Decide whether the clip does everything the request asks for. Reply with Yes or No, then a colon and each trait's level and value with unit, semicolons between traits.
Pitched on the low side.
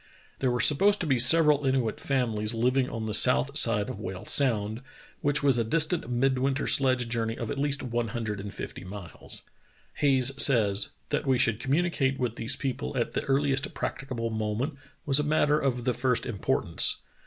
Yes: low, 125 Hz